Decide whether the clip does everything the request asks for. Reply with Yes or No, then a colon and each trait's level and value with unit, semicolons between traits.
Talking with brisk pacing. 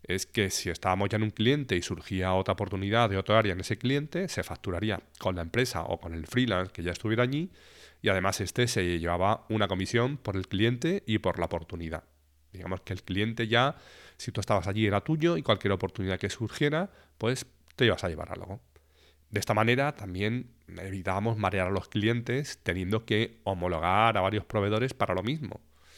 Yes: fast, 195 wpm